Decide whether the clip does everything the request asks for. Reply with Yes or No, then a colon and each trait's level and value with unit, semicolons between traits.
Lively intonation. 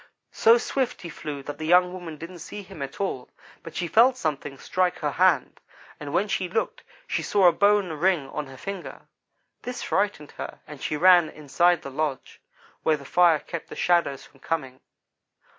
No: average, 3.9 semitones